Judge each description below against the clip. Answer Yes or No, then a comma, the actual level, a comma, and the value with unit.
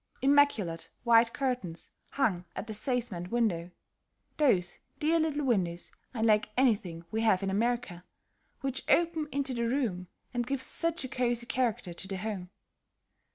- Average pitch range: No, wide, 5.8 semitones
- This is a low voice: No, high, 235 Hz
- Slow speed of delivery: No, average, 145 wpm